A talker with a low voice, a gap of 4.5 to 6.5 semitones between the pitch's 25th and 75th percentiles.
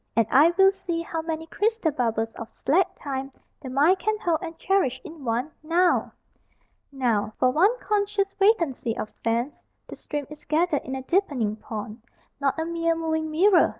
No: very high, 315 Hz; wide, 5.6 semitones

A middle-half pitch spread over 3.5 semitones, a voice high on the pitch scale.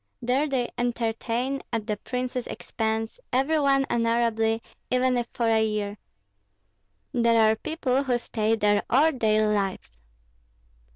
No: narrow, 2.5 semitones; high, 235 Hz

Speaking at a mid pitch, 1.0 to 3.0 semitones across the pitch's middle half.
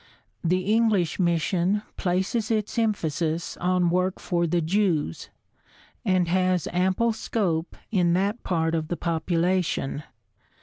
Yes: medium, 180 Hz; narrow, 2.6 semitones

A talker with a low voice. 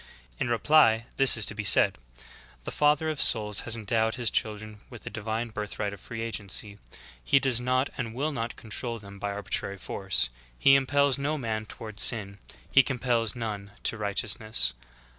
Yes: low, 115 Hz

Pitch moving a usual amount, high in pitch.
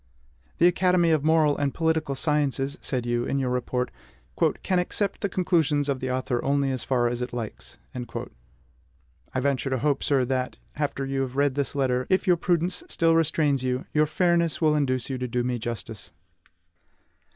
No: average, 3.9 semitones; low, 135 Hz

